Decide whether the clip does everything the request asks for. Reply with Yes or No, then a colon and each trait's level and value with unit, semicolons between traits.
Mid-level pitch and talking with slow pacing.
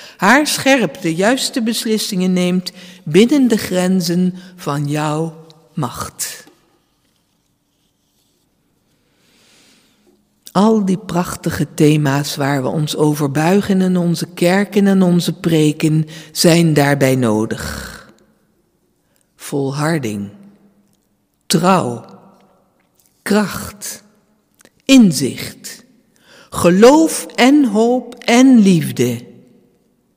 Yes: medium, 180 Hz; slow, 80 wpm